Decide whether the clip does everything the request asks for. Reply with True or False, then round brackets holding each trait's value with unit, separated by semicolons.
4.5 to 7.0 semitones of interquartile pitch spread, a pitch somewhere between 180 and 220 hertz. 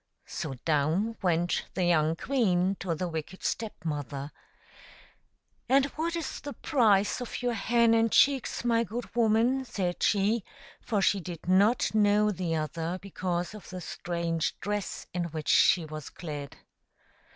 True (5.3 semitones; 190 Hz)